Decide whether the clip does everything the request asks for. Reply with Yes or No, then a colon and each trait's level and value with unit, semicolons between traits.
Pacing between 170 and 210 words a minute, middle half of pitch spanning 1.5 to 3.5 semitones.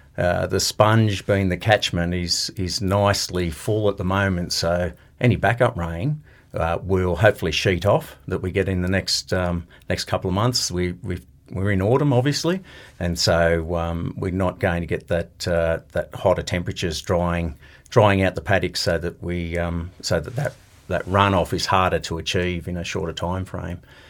Yes: average, 185 wpm; narrow, 2.5 semitones